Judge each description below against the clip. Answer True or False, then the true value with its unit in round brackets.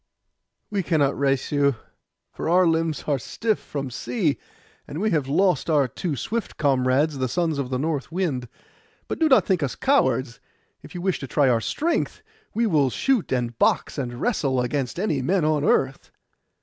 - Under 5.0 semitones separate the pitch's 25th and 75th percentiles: False (5.5 semitones)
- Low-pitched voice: False (150 Hz)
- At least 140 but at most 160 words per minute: False (185 wpm)